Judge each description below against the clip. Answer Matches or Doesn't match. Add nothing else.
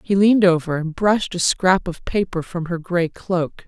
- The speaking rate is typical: Doesn't match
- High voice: Doesn't match